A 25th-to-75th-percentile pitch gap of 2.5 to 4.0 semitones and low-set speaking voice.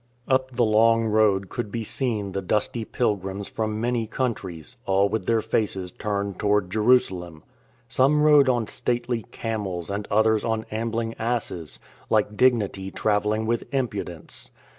Yes: average, 2.8 semitones; low, 110 Hz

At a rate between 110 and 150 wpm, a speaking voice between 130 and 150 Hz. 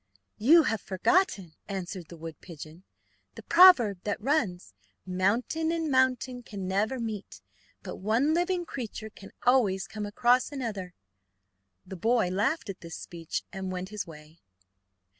No: average, 140 wpm; high, 210 Hz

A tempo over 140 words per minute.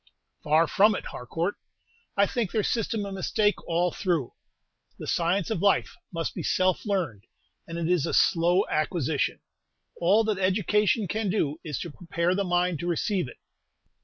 Yes: average, 165 wpm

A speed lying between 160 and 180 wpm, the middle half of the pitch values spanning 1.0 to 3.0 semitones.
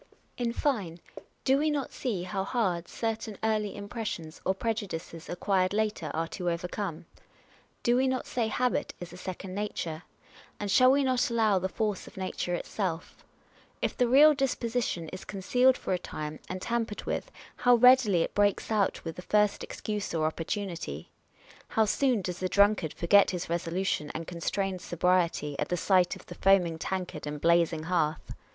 No: average, 170 wpm; average, 4.6 semitones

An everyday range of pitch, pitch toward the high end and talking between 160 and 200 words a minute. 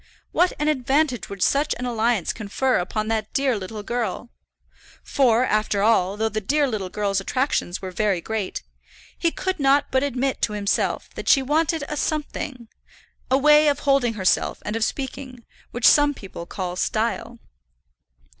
Yes: average, 5.0 semitones; high, 240 Hz; average, 165 wpm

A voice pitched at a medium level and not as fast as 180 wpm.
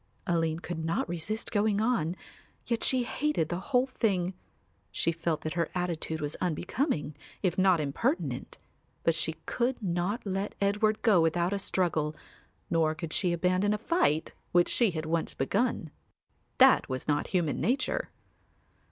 Yes: medium, 180 Hz; average, 150 wpm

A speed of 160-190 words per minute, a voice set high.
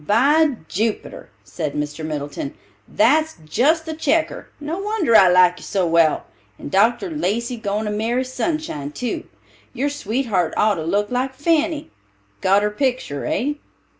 No: average, 150 wpm; high, 235 Hz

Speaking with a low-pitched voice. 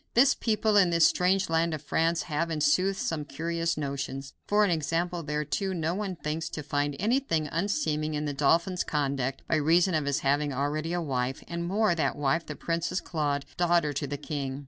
No: medium, 160 Hz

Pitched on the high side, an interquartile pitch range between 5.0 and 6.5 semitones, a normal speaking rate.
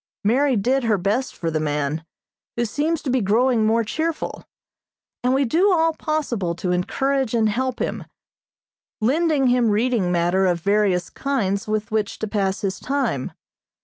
Yes: high, 225 Hz; wide, 5.6 semitones; average, 160 wpm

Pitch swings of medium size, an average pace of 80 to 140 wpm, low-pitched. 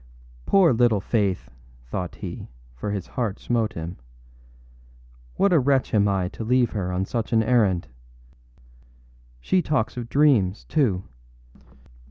Yes: average, 4.7 semitones; slow, 135 wpm; low, 110 Hz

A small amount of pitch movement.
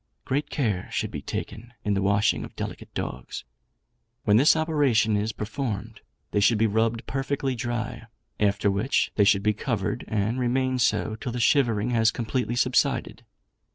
No: average, 3.3 semitones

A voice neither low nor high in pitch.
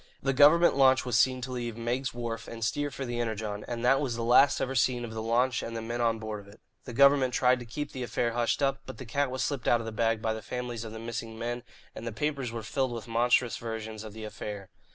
No: low, 120 Hz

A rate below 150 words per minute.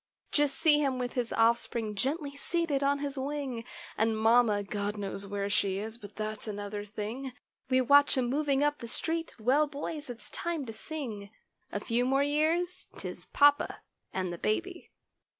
No: average, 155 wpm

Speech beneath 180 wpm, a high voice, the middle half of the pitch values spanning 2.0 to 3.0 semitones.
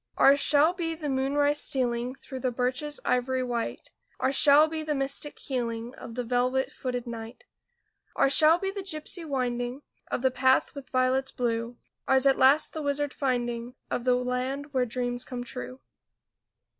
Yes: average, 170 wpm; very high, 260 Hz; average, 2.7 semitones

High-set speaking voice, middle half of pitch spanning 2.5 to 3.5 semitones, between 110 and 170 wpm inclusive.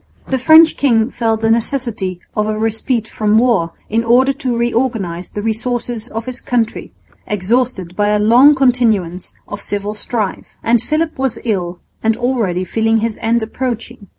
Yes: high, 225 Hz; average, 2.9 semitones; average, 160 wpm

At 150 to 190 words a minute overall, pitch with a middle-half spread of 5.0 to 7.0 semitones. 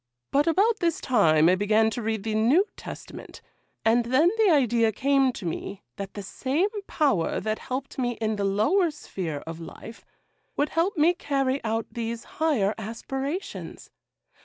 Yes: average, 160 wpm; wide, 5.5 semitones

